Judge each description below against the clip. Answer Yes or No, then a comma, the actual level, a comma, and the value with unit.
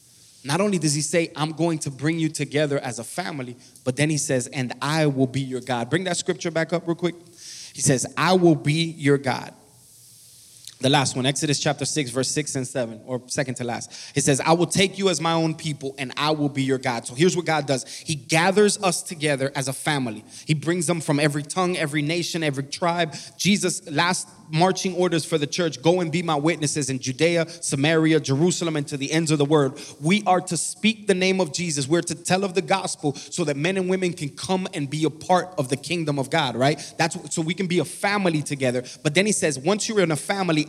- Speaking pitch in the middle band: Yes, medium, 155 Hz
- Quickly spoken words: Yes, fast, 240 wpm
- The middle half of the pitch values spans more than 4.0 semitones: No, average, 3.6 semitones